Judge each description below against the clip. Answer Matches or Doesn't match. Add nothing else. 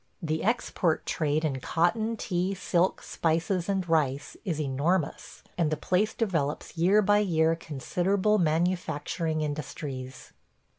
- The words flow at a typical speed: Doesn't match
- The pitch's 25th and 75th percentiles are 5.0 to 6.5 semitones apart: Doesn't match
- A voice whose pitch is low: Doesn't match